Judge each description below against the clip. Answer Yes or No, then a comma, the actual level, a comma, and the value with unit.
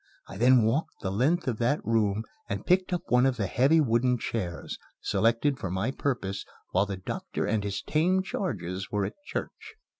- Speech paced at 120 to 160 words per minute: No, average, 185 wpm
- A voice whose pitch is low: Yes, low, 115 Hz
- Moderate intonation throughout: No, wide, 6.2 semitones